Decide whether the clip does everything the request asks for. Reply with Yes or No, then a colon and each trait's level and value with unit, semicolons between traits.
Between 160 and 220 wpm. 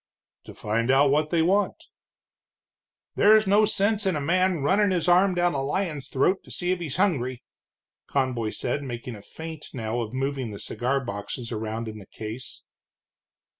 Yes: average, 170 wpm